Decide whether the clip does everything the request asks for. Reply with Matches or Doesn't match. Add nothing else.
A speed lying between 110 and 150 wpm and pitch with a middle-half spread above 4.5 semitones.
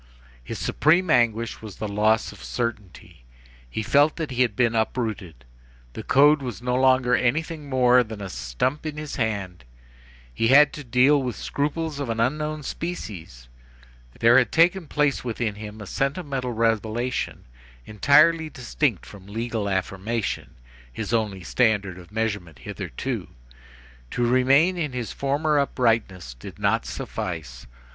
Matches